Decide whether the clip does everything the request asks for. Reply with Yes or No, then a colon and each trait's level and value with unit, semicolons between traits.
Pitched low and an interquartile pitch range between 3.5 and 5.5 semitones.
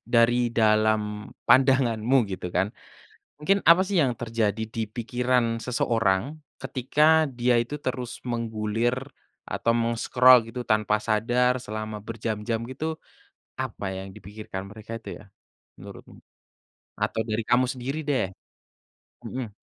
No: low, 115 Hz; average, 2.8 semitones